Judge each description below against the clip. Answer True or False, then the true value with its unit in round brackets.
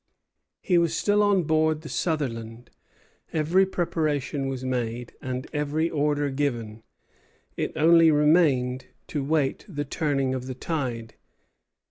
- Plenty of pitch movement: False (3.7 semitones)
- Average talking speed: False (125 wpm)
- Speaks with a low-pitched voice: False (145 Hz)